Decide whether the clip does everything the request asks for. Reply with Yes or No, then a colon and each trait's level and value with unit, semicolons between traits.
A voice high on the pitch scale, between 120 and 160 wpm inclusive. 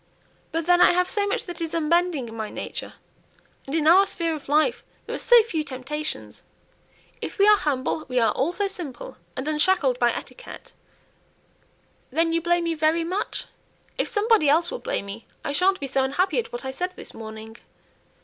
No: very high, 320 Hz; average, 190 wpm